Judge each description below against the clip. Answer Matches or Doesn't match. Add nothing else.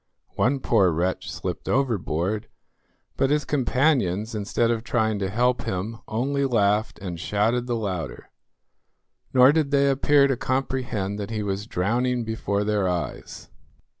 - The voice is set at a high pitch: Doesn't match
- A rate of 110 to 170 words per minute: Matches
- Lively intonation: Doesn't match